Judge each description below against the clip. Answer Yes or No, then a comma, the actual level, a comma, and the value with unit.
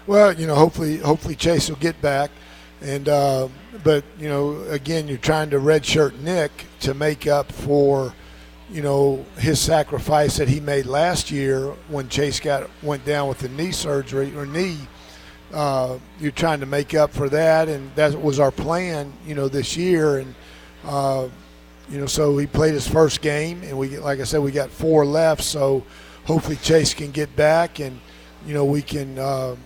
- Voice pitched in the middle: Yes, medium, 145 Hz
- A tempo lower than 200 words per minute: Yes, average, 185 wpm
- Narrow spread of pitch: Yes, narrow, 2.2 semitones